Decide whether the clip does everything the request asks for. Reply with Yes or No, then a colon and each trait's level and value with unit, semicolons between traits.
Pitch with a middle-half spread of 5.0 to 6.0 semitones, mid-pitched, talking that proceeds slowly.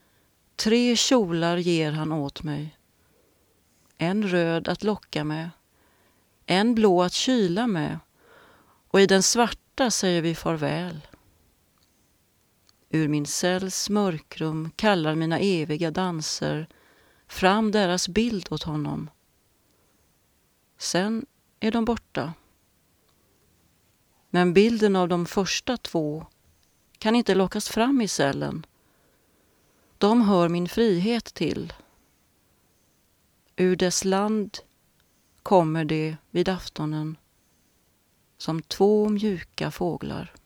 Yes: wide, 5.4 semitones; medium, 175 Hz; slow, 100 wpm